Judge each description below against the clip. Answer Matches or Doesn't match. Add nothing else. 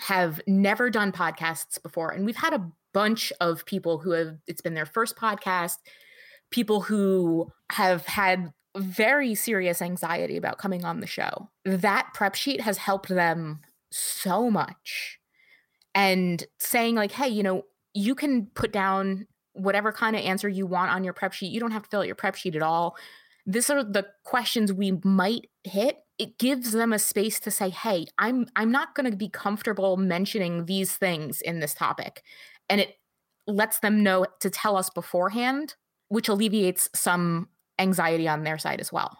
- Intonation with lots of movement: Doesn't match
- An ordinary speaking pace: Matches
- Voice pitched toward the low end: Doesn't match